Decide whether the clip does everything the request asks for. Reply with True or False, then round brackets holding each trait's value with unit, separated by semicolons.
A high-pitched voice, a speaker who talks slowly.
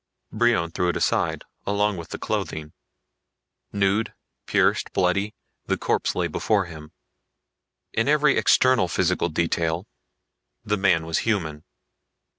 False (95 Hz; 120 wpm)